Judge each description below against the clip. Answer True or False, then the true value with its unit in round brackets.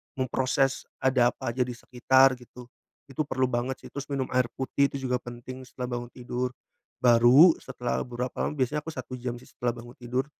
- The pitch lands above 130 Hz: False (125 Hz)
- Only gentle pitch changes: True (1.5 semitones)